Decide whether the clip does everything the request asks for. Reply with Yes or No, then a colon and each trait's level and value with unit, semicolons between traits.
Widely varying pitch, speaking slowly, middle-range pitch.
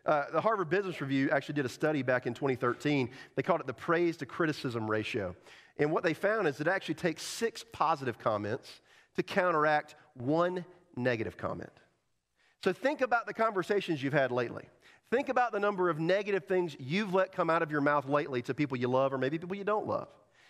No: wide, 5.7 semitones; fast, 205 wpm; medium, 160 Hz